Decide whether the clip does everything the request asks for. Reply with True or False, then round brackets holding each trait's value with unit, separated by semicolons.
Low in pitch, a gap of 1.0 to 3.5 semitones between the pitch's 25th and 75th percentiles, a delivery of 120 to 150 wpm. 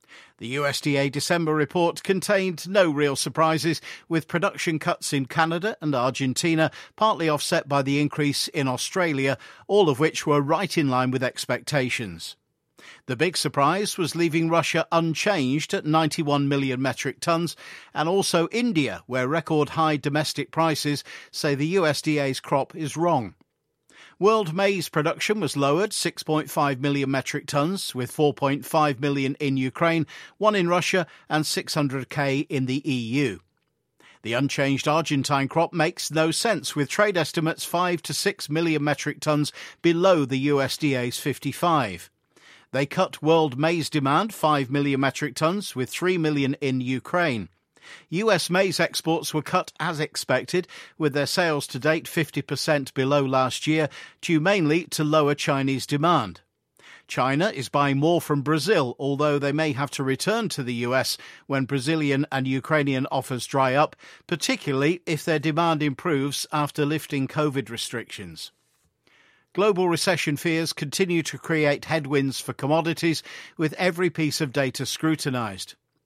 False (150 Hz; 3.1 semitones; 145 wpm)